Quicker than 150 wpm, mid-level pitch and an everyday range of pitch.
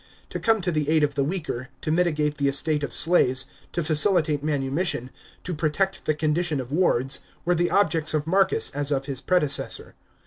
Yes: average, 185 wpm; medium, 155 Hz; average, 3.6 semitones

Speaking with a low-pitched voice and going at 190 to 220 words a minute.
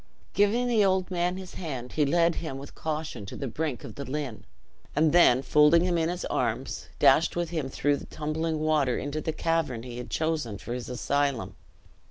No: medium, 155 Hz; average, 200 wpm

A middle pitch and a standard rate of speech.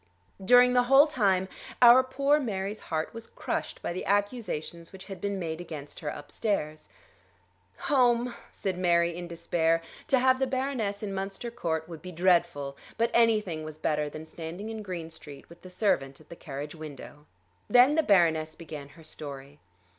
Yes: medium, 180 Hz; average, 170 wpm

